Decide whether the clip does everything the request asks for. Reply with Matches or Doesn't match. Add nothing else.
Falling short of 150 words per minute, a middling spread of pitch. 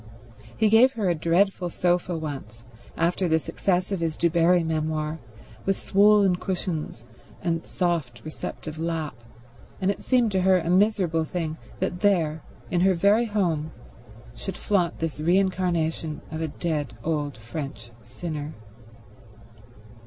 Matches